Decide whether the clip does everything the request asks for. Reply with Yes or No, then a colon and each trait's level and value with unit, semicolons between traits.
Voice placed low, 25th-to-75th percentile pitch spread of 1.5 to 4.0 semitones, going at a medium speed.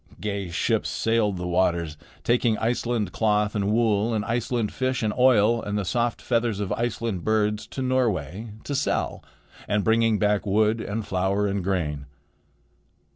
Yes: low, 105 Hz; average, 2.7 semitones; average, 155 wpm